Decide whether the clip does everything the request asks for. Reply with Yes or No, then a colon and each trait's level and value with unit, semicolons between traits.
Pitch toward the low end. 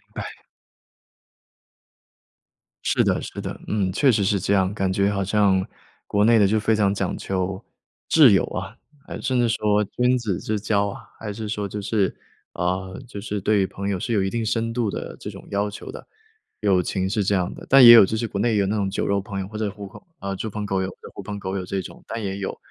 Yes: low, 100 Hz